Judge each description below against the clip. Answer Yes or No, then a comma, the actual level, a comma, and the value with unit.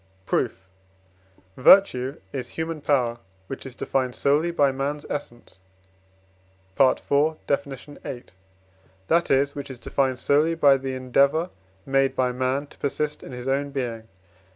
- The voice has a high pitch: No, low, 135 Hz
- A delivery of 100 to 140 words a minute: Yes, slow, 135 wpm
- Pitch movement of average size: No, narrow, 2.1 semitones